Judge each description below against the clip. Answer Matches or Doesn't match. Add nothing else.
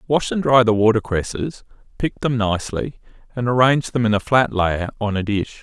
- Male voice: Matches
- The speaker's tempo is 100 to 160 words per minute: Doesn't match